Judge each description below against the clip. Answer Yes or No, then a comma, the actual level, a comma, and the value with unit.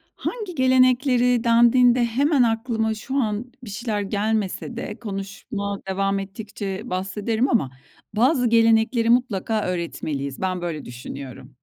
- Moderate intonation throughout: Yes, average, 3.9 semitones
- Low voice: No, high, 220 Hz